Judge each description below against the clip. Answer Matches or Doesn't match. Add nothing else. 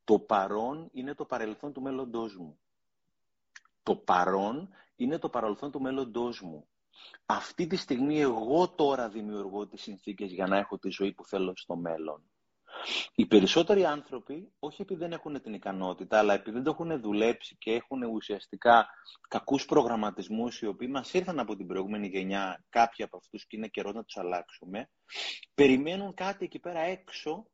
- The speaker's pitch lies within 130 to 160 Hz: Doesn't match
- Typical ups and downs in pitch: Doesn't match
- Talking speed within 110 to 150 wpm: Doesn't match